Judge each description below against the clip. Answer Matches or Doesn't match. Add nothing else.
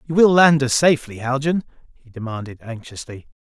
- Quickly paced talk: Doesn't match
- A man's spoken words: Matches